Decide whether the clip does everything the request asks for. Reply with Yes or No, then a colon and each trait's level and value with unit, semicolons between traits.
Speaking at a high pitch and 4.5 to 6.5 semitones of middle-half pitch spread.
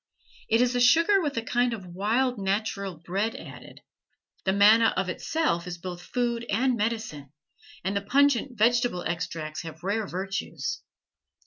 Yes: high, 215 Hz; average, 4.9 semitones